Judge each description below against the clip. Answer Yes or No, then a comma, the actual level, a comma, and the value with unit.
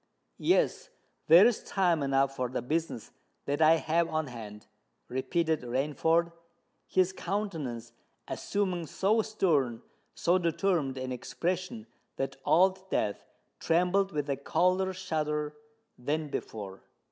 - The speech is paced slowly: Yes, slow, 110 wpm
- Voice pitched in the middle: Yes, medium, 160 Hz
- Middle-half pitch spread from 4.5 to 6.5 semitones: Yes, average, 5.2 semitones